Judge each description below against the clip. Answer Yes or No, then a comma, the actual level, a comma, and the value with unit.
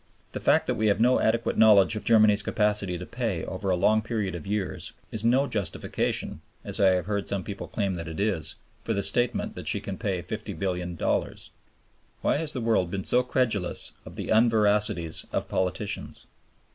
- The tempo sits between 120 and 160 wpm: No, average, 185 wpm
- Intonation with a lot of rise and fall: No, average, 3.0 semitones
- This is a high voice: No, low, 105 Hz